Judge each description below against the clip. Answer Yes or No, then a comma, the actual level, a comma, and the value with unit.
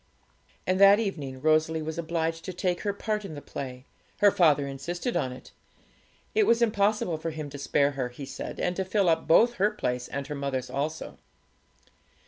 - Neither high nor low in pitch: Yes, medium, 160 Hz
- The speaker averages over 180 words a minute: Yes, average, 190 wpm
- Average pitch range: No, wide, 5.8 semitones